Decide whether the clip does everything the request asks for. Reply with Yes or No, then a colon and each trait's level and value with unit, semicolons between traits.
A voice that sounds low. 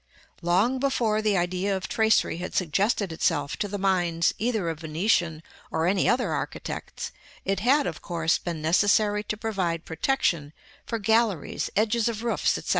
No: high, 195 Hz